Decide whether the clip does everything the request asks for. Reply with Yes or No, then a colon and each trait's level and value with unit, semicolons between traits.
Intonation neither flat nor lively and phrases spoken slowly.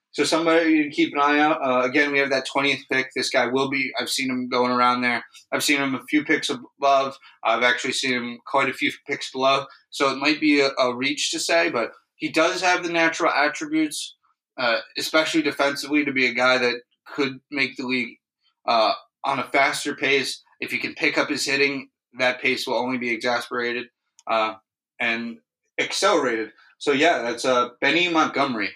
No: average, 3.1 semitones; average, 200 wpm